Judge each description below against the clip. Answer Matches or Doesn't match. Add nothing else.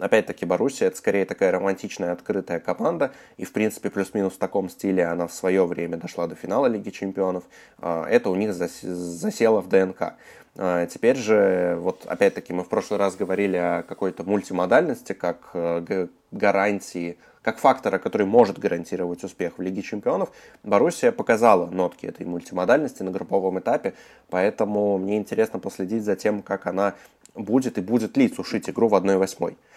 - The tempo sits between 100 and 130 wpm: Doesn't match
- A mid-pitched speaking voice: Doesn't match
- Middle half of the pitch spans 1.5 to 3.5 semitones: Matches